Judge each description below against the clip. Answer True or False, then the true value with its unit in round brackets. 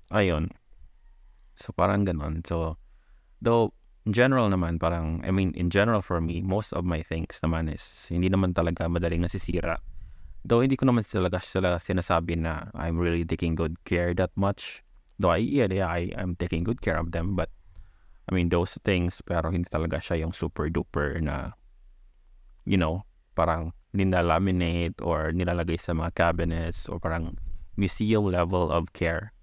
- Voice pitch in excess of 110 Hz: False (85 Hz)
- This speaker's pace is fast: True (170 wpm)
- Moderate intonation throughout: False (2.2 semitones)